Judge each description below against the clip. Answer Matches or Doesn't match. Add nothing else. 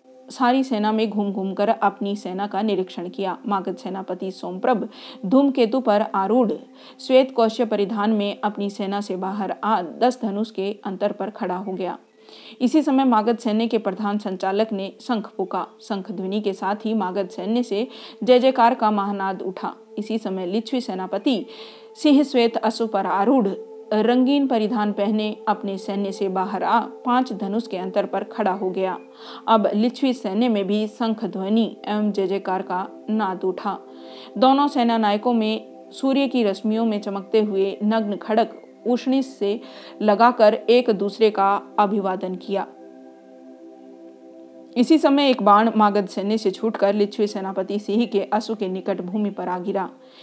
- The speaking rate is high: Doesn't match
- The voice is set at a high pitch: Matches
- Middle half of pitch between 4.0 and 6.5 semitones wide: Doesn't match